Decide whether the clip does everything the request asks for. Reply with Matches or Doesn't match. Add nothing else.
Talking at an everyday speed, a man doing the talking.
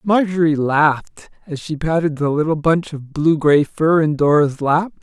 Matches